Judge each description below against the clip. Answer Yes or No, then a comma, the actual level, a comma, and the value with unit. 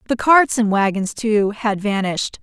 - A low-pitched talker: No, high, 215 Hz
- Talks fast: No, average, 175 wpm